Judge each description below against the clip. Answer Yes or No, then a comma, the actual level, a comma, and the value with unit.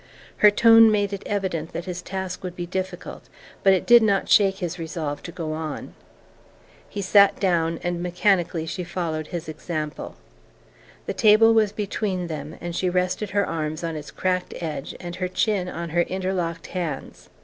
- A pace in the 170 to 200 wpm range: Yes, average, 175 wpm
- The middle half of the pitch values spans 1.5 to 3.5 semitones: Yes, average, 2.9 semitones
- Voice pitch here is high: No, medium, 180 Hz